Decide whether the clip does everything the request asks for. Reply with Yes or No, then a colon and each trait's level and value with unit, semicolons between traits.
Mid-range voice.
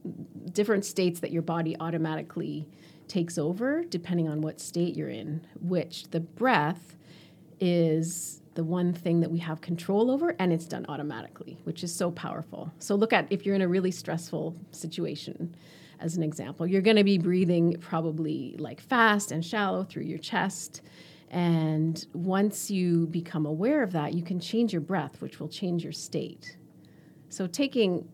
Yes: medium, 170 Hz